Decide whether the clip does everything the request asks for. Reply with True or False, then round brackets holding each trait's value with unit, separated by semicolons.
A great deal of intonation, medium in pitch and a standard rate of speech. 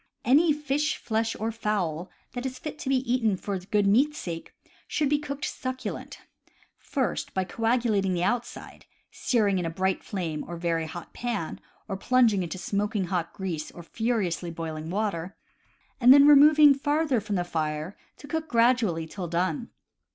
False (6.5 semitones; 210 Hz; 175 wpm)